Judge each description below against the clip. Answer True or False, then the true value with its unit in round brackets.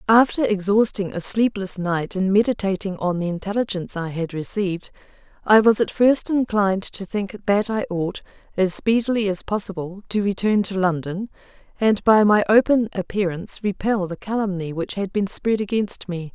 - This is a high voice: True (200 Hz)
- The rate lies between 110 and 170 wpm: True (165 wpm)